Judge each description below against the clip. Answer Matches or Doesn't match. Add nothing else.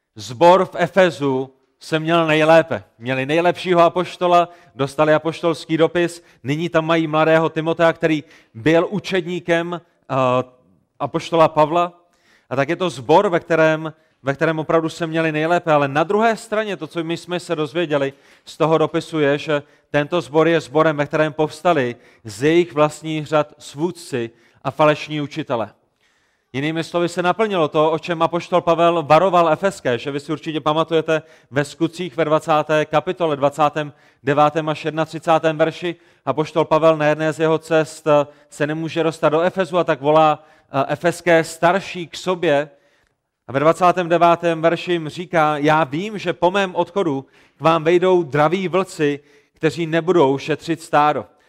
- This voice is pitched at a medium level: Matches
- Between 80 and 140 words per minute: Doesn't match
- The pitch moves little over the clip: Matches